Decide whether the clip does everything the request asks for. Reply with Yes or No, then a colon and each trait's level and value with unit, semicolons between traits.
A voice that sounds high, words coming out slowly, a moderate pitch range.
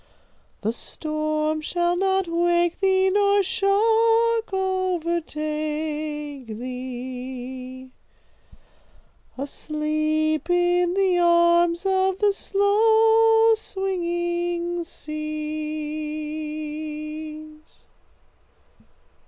Yes: very high, 335 Hz; slow, 60 wpm; average, 3.8 semitones